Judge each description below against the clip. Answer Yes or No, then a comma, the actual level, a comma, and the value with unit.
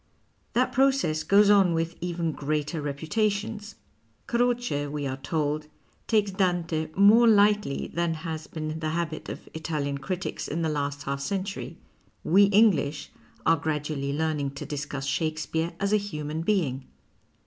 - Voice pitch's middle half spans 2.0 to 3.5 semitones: No, average, 5.2 semitones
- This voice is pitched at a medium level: Yes, medium, 160 Hz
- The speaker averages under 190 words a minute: Yes, average, 140 wpm